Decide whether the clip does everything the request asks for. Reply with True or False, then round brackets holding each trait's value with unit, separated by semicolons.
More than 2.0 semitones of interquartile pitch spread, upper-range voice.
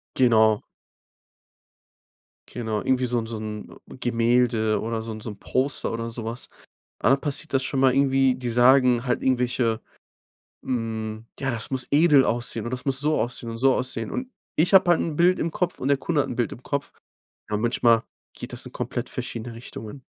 False (2.9 semitones; 125 Hz)